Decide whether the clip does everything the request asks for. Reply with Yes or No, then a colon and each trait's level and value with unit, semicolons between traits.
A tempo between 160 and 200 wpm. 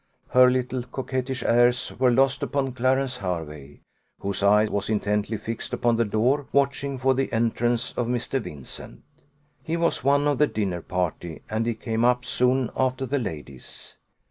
Yes: average, 165 wpm